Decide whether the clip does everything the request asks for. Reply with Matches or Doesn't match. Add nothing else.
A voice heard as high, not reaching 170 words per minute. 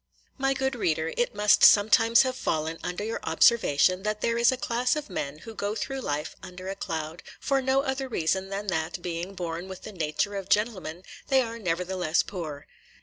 Doesn't match